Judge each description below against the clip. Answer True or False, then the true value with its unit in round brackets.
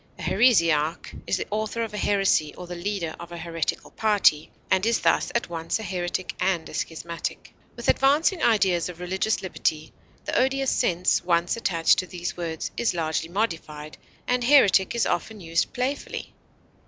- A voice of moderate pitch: True (180 Hz)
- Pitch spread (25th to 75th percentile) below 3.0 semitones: False (4.7 semitones)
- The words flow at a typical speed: True (170 wpm)